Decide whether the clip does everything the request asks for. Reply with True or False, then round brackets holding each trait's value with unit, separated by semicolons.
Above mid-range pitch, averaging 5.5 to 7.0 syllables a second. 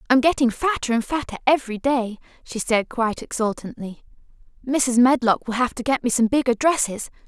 True (245 Hz; 5.6 syllables/s)